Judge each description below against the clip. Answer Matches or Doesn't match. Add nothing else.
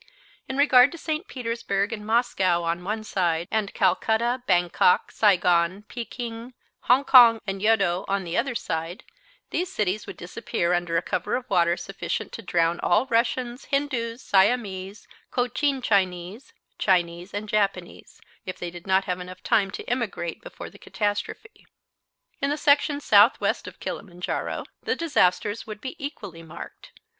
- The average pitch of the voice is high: Matches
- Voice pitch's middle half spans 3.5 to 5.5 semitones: Matches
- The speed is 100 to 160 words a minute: Matches